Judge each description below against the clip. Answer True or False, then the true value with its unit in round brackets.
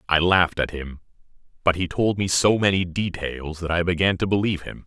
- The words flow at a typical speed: False (210 wpm)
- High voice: False (90 Hz)